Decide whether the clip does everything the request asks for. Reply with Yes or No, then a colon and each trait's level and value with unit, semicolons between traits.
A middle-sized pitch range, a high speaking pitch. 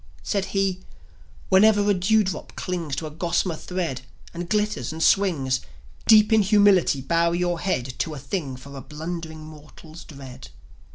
No: average, 4.4 semitones; medium, 170 Hz